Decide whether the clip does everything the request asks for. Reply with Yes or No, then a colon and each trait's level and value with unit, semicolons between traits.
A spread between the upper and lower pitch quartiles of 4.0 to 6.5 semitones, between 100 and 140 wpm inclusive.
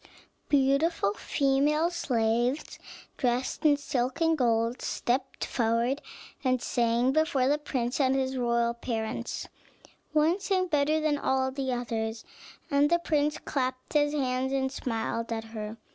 No: average, 3.6 semitones; slow, 135 wpm